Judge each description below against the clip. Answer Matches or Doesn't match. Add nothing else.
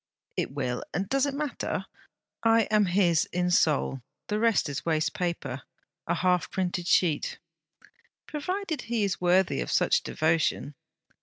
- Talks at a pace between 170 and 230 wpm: Doesn't match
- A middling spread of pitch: Doesn't match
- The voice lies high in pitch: Doesn't match